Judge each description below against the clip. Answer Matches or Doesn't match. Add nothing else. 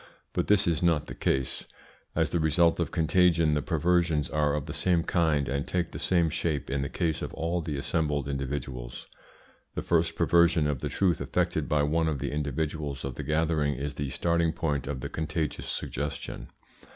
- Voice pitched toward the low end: Matches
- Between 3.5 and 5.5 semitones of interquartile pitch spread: Doesn't match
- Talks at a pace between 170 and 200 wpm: Matches